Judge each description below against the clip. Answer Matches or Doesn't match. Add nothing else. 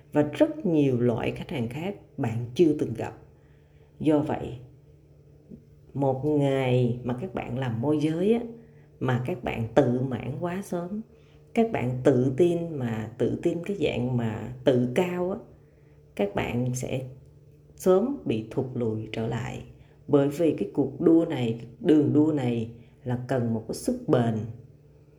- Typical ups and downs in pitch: Matches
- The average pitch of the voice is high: Doesn't match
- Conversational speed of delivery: Doesn't match